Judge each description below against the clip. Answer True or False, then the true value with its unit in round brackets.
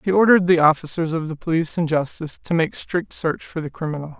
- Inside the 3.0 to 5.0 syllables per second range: False (6.4 syllables/s)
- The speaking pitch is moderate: True (165 Hz)